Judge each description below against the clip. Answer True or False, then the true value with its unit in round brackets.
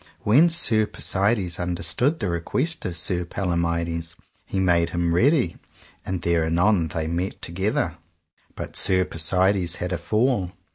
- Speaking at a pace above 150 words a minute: False (140 wpm)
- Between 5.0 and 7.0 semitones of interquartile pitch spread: False (3.2 semitones)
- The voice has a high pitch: False (90 Hz)